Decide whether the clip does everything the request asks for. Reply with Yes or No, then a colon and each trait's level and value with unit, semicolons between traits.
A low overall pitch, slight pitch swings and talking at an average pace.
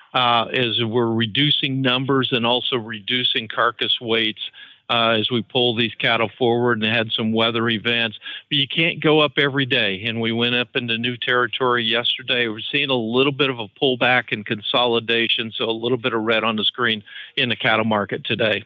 Yes: low, 120 Hz; narrow, 2.1 semitones; average, 195 wpm